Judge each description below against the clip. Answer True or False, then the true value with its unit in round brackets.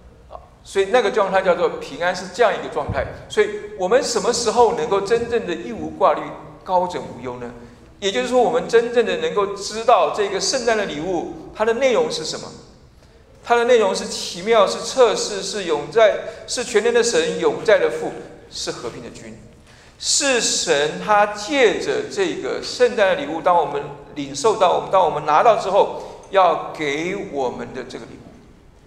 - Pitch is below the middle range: False (235 Hz)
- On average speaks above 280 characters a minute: False (265 characters per minute)